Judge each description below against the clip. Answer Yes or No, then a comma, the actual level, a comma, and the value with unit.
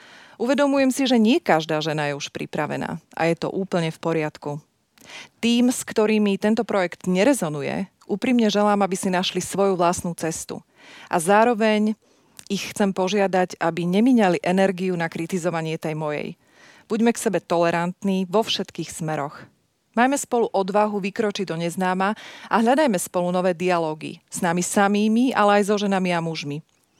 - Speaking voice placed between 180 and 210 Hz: Yes, high, 190 Hz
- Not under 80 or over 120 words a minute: No, average, 150 wpm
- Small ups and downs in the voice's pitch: No, average, 4.0 semitones